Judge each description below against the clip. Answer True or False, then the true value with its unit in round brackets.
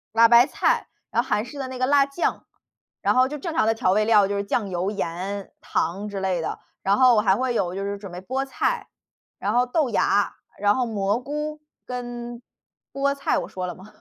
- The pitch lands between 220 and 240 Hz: True (225 Hz)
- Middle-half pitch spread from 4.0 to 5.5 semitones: True (4.5 semitones)